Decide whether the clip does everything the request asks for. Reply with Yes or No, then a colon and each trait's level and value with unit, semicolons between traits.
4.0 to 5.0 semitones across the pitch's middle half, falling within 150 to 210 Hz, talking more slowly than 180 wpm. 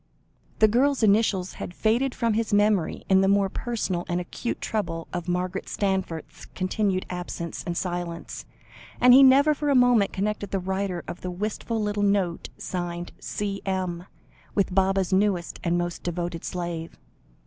No: average, 3.2 semitones; high, 190 Hz; average, 155 wpm